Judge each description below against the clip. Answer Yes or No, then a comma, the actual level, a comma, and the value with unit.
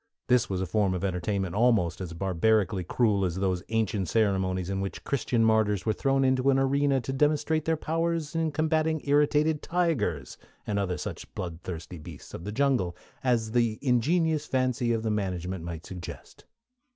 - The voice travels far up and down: Yes, wide, 6.9 semitones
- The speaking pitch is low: Yes, low, 110 Hz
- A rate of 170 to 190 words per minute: Yes, average, 175 wpm